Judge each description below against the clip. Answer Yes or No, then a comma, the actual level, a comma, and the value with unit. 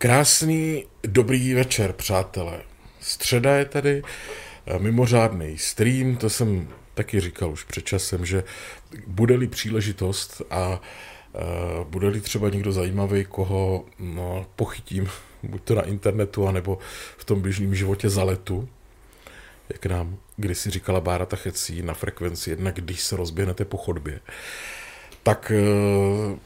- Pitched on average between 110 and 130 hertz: No, low, 100 Hz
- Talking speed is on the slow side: No, average, 125 wpm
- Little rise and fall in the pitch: No, average, 3.0 semitones